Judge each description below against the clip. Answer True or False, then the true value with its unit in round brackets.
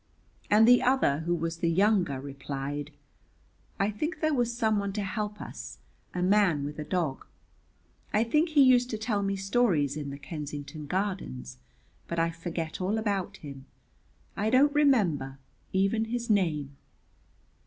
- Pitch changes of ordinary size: False (6.9 semitones)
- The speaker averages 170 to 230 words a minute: False (155 wpm)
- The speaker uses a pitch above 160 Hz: True (190 Hz)